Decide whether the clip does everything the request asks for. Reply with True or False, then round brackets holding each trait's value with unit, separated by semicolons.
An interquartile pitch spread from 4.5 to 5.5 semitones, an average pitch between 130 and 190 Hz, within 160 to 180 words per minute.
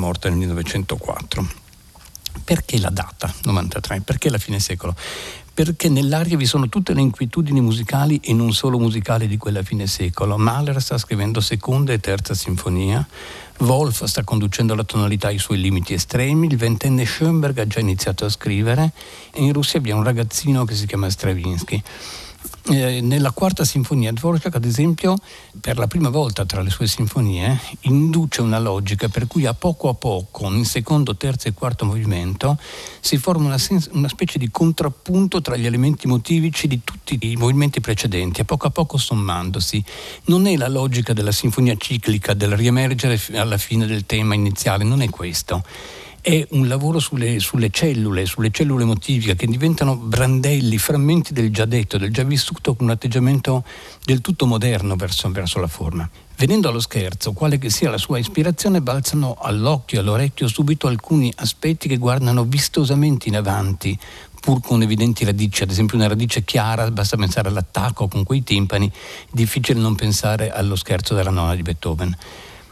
False (5.1 semitones; 120 Hz; 170 wpm)